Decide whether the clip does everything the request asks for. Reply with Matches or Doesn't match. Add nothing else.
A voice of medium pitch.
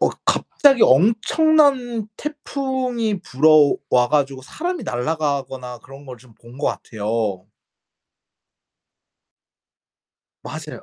Matches